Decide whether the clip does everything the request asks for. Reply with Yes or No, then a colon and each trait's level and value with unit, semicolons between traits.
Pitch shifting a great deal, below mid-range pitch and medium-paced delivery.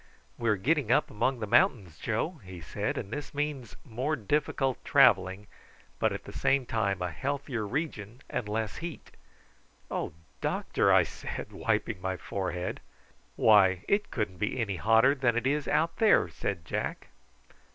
Yes: wide, 6.1 semitones; low, 115 Hz; average, 160 wpm